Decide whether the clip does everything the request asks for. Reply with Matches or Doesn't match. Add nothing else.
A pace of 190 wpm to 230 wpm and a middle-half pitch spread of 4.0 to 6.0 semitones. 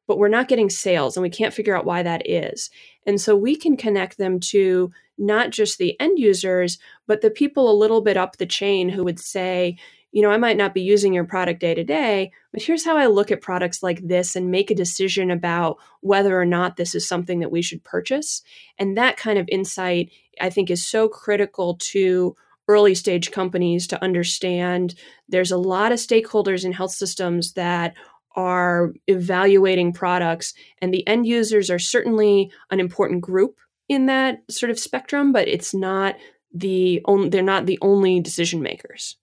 Doesn't match